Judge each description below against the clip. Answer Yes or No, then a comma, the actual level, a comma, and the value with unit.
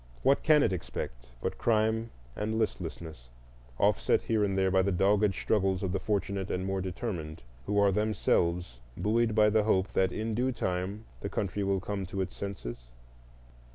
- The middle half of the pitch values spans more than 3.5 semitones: No, narrow, 2.6 semitones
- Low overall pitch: Yes, low, 100 Hz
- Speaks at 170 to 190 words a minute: Yes, average, 175 wpm